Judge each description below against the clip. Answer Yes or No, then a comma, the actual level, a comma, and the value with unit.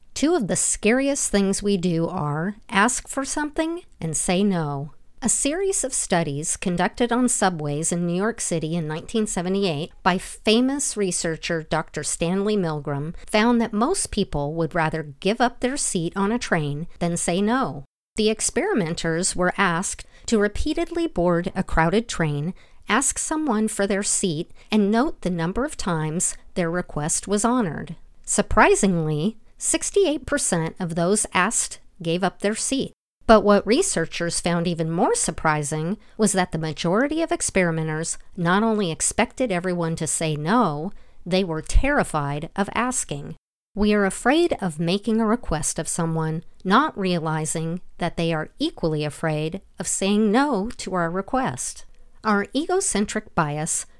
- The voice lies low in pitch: No, high, 190 Hz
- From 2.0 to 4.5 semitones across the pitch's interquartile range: No, average, 5.2 semitones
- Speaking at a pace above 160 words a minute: No, average, 150 wpm